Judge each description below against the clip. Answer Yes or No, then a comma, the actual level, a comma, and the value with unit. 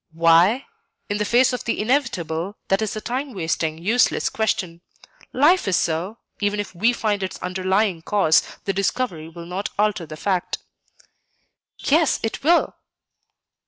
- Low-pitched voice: No, high, 200 Hz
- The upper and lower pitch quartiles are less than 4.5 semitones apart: No, average, 4.9 semitones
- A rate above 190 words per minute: No, average, 150 wpm